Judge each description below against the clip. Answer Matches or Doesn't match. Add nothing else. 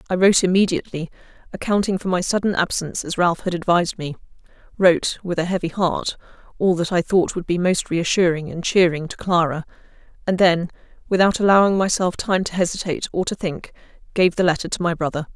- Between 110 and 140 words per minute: Doesn't match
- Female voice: Matches